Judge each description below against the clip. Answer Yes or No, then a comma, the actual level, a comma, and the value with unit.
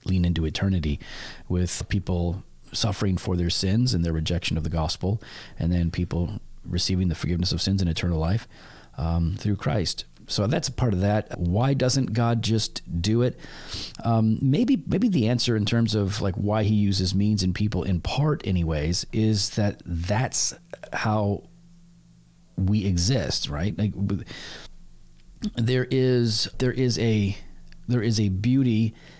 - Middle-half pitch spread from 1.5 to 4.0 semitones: No, average, 4.8 semitones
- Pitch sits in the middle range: No, low, 100 Hz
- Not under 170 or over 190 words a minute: No, average, 155 wpm